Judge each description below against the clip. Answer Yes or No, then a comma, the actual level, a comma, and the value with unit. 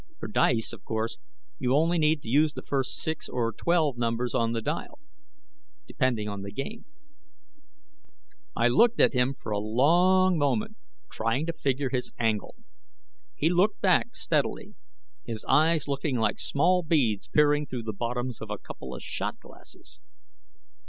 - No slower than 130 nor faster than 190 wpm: Yes, average, 160 wpm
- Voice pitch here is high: No, low, 135 Hz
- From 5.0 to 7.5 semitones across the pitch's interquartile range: Yes, wide, 5.4 semitones